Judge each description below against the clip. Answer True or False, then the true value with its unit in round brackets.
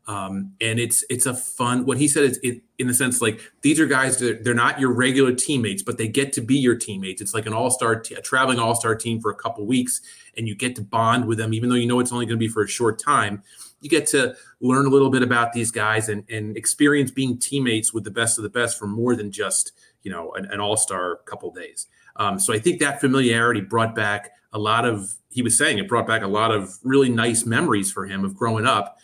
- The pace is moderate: False (260 wpm)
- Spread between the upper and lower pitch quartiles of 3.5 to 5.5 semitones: False (2.8 semitones)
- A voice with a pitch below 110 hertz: False (120 Hz)